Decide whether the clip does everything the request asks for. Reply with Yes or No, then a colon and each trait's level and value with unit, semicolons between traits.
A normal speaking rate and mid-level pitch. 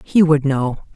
Yes: average, 190 wpm; medium, 150 Hz